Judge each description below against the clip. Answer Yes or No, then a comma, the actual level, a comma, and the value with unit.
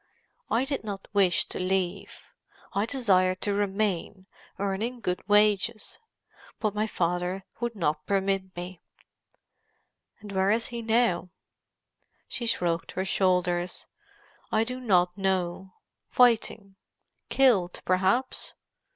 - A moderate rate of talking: No, slow, 115 wpm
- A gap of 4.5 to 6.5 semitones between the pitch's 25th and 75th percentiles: No, average, 3.2 semitones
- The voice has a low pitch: No, high, 195 Hz